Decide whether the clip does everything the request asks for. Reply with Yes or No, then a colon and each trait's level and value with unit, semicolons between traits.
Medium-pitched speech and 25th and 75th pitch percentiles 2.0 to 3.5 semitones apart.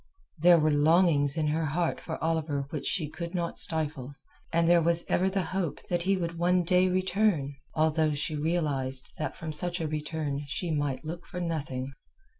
Yes: medium, 160 Hz; average, 2.8 semitones